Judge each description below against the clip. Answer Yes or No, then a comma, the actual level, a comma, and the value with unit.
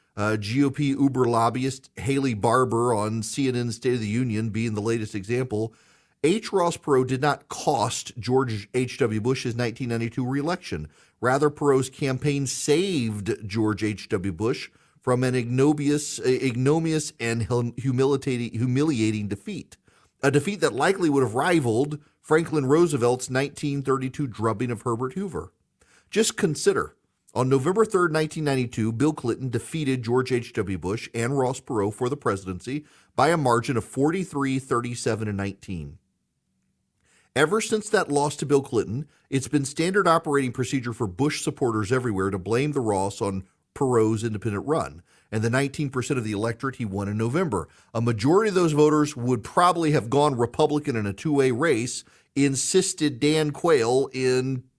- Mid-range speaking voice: No, low, 130 Hz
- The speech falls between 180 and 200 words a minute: No, average, 145 wpm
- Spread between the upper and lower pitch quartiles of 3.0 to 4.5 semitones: Yes, average, 4.1 semitones